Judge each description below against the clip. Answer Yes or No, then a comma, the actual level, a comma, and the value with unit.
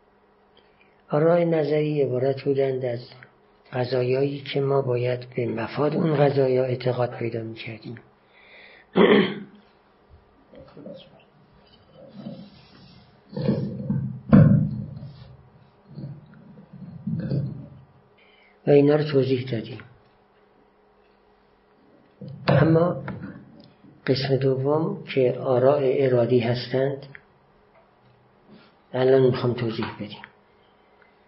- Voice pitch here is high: No, low, 135 Hz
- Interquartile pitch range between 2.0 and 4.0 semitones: Yes, average, 3.3 semitones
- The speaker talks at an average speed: No, slow, 60 wpm